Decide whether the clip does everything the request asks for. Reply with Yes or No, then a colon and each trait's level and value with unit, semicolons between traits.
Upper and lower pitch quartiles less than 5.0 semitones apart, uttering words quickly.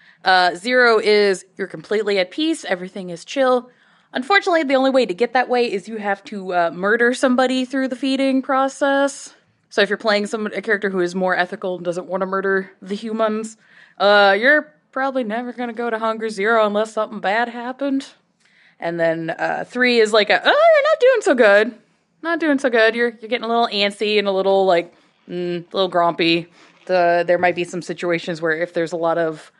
No: wide, 5.5 semitones; fast, 210 wpm